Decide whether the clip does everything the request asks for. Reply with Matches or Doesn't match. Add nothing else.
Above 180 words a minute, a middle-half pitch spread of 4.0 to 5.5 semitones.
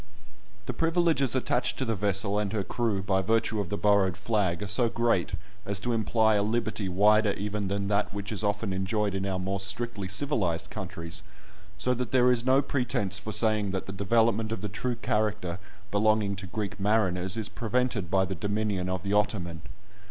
Doesn't match